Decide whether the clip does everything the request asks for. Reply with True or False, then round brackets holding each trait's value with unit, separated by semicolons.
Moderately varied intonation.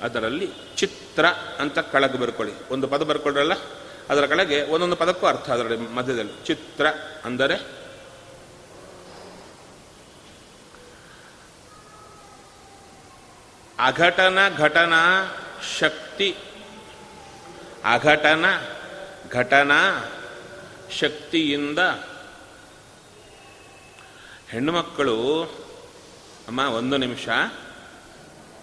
True (4.6 semitones)